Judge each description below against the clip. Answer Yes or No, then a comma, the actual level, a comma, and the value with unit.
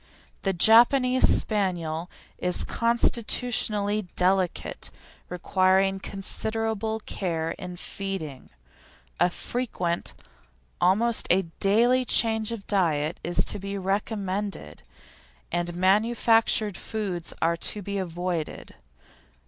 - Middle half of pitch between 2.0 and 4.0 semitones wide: Yes, average, 3.7 semitones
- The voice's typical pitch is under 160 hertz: No, high, 195 Hz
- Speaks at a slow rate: Yes, slow, 90 wpm